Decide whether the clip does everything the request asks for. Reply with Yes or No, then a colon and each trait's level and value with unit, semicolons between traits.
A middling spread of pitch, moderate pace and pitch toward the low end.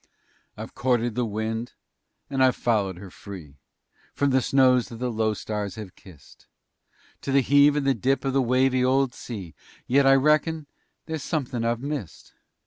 Yes: average, 3.8 semitones; average, 170 wpm; low, 125 Hz